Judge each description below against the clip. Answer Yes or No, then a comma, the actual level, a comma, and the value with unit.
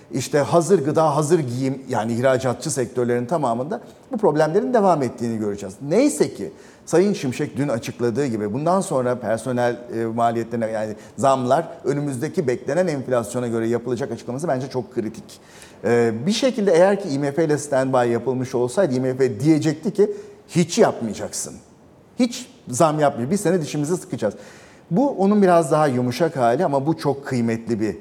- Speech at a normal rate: No, fast, 150 wpm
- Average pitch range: No, wide, 5.9 semitones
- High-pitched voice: No, low, 135 Hz